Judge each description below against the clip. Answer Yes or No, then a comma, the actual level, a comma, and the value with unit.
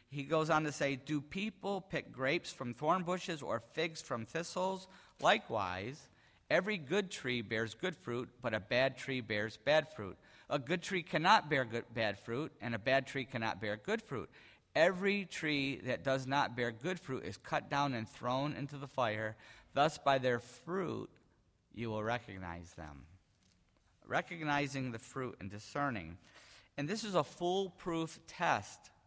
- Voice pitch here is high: No, low, 135 Hz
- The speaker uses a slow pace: No, average, 165 wpm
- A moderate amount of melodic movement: No, wide, 5.9 semitones